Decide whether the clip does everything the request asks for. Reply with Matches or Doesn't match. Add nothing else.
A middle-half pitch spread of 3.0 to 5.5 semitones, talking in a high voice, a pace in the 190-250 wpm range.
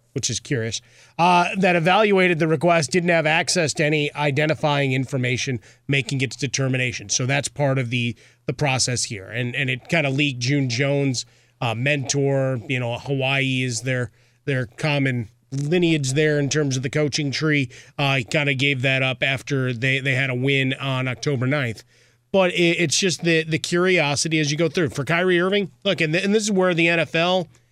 Doesn't match